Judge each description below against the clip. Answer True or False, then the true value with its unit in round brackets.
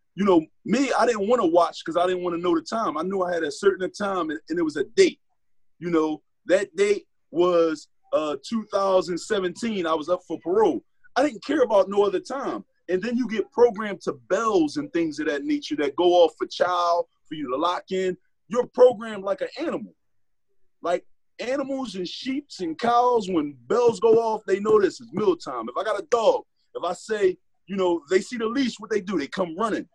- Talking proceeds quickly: True (220 wpm)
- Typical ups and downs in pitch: False (9.0 semitones)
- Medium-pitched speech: False (225 Hz)